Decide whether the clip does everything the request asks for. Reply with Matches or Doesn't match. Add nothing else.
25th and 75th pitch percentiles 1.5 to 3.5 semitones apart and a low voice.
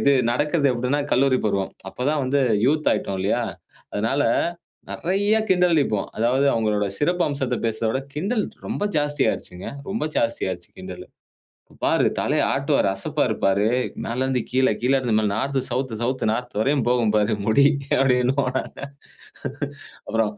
Doesn't match